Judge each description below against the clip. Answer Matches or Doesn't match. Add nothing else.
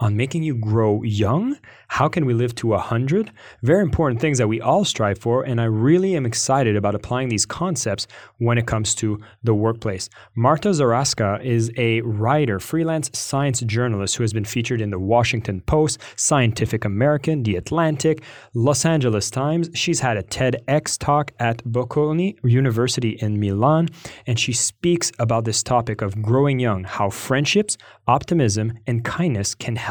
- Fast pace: Doesn't match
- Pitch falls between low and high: Doesn't match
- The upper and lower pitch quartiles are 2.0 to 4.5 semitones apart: Doesn't match